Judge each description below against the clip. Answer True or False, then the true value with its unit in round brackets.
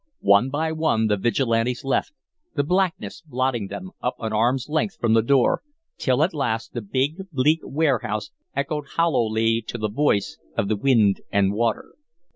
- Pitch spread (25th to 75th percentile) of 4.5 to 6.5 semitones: True (5.1 semitones)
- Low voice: True (125 Hz)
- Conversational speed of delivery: True (165 wpm)